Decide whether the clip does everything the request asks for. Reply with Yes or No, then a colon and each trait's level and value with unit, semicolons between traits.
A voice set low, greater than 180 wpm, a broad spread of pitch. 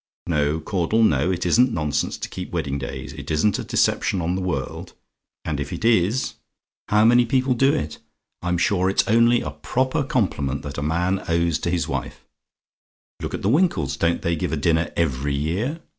Yes: very low, 90 Hz; average, 190 wpm; wide, 6.7 semitones